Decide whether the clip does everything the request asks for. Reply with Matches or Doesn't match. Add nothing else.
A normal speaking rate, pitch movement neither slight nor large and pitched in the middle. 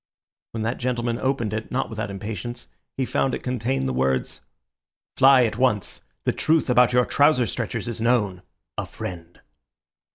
Doesn't match